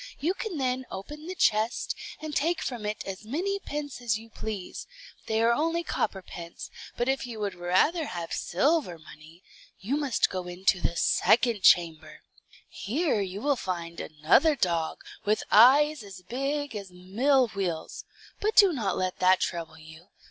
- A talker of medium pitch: No, high, 215 Hz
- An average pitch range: No, wide, 7.8 semitones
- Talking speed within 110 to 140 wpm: No, average, 165 wpm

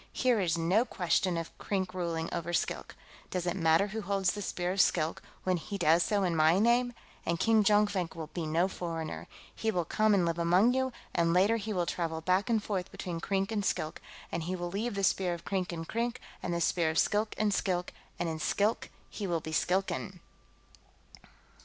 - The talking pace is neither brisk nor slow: No, fast, 210 wpm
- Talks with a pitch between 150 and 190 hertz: Yes, medium, 185 Hz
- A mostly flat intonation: No, average, 3.4 semitones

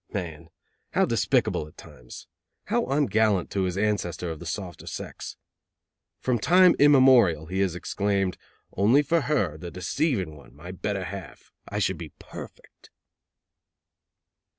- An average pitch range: No, wide, 5.9 semitones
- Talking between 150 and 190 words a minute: No, slow, 135 wpm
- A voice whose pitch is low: Yes, very low, 95 Hz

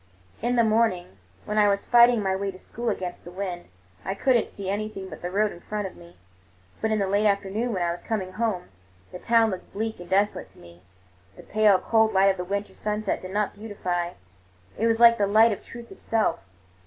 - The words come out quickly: Yes, fast, 220 wpm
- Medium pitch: No, high, 200 Hz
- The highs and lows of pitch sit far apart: No, average, 3.1 semitones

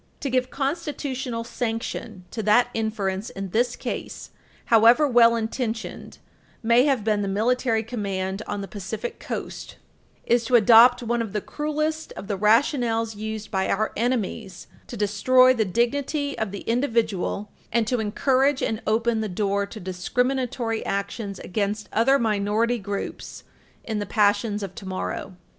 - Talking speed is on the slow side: No, average, 150 wpm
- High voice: Yes, high, 225 Hz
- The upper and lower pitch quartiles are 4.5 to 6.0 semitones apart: No, average, 3.2 semitones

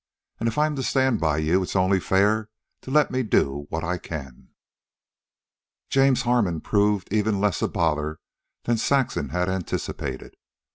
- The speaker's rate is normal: Yes, average, 155 wpm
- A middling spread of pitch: No, wide, 6.7 semitones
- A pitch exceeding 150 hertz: No, low, 100 Hz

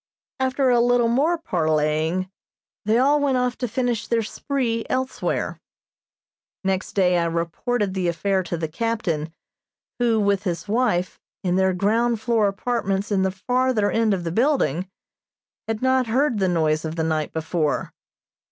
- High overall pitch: Yes, high, 205 Hz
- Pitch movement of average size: No, wide, 5.7 semitones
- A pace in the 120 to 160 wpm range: Yes, average, 155 wpm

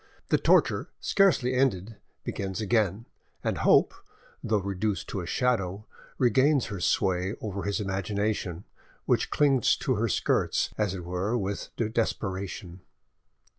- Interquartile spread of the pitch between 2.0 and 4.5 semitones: Yes, average, 3.4 semitones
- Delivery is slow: Yes, slow, 130 wpm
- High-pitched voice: No, low, 100 Hz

